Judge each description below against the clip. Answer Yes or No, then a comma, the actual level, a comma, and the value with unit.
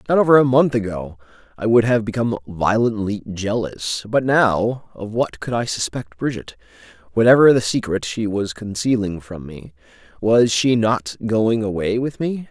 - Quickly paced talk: No, average, 165 wpm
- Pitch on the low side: Yes, low, 110 Hz